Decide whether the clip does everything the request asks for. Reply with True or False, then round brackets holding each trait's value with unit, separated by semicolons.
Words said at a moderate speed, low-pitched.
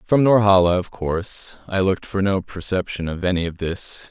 True (190 wpm; 95 Hz)